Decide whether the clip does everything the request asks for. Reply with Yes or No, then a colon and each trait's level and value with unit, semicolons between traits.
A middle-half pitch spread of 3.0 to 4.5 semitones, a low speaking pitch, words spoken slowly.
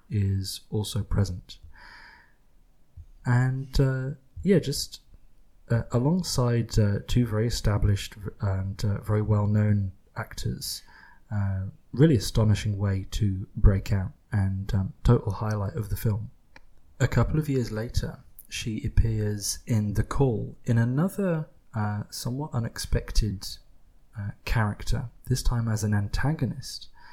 Yes: average, 3.6 semitones; low, 110 Hz; slow, 120 wpm